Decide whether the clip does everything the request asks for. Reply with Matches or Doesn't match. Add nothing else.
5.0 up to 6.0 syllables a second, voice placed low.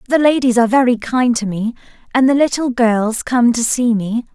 Doesn't match